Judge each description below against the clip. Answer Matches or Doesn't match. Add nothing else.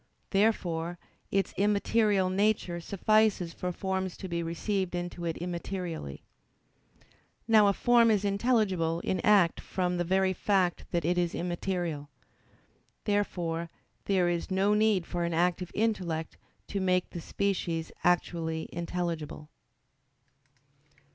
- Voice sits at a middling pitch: Matches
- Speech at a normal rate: Doesn't match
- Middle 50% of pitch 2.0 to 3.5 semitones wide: Matches